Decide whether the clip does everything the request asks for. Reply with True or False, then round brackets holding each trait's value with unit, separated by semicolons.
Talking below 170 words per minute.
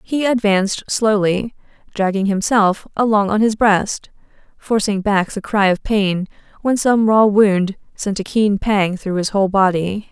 True (160 wpm)